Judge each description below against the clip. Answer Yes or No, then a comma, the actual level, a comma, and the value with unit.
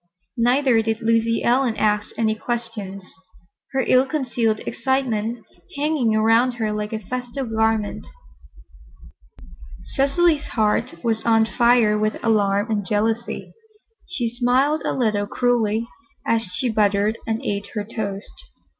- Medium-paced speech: No, slow, 125 wpm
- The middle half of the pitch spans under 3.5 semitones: Yes, narrow, 2.5 semitones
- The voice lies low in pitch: No, high, 225 Hz